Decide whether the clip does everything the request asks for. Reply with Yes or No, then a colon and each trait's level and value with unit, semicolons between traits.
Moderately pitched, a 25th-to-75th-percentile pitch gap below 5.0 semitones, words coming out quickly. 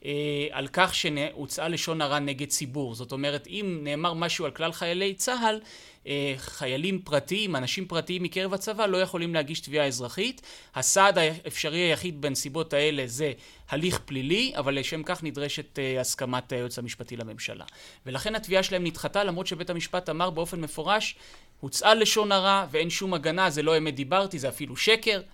Yes: medium, 160 Hz; average, 4.6 semitones; fast, 155 wpm